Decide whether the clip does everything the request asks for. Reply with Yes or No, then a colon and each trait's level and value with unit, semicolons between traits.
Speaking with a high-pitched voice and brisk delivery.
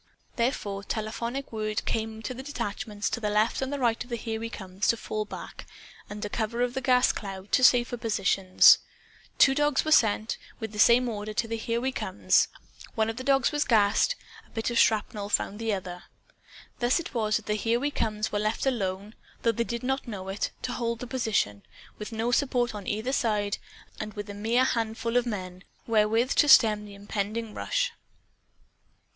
No: high, 225 Hz; average, 195 wpm